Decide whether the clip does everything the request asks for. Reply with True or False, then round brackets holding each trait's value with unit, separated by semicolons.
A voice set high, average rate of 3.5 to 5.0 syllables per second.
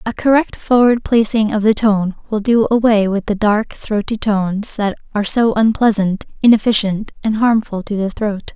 True (215 Hz; 4.9 syllables/s)